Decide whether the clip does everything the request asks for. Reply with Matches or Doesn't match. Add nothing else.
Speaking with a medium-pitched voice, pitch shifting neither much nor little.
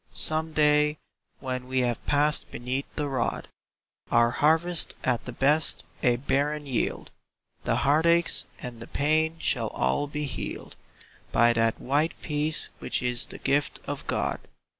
Matches